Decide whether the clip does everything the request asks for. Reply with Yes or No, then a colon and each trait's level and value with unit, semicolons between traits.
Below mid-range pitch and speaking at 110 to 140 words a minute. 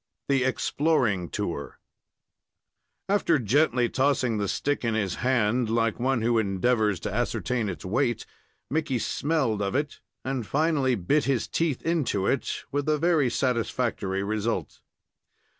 Yes: low, 125 Hz; slow, 135 wpm